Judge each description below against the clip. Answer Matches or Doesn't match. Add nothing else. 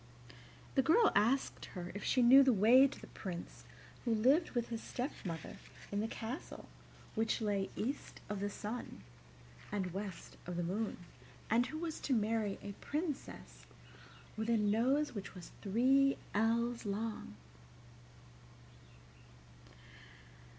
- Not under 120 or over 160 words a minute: Matches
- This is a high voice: Matches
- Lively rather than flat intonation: Doesn't match